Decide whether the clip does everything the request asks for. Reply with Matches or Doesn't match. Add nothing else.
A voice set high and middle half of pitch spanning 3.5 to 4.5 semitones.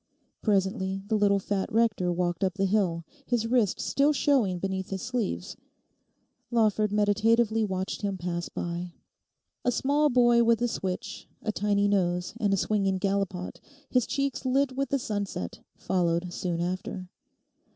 Matches